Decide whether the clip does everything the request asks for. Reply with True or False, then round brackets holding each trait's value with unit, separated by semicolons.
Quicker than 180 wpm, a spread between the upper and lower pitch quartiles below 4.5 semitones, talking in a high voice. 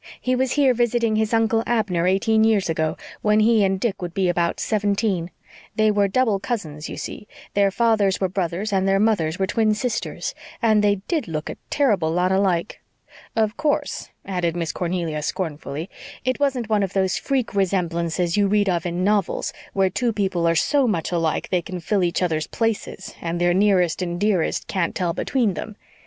True (190 wpm; 3.9 semitones; 195 Hz)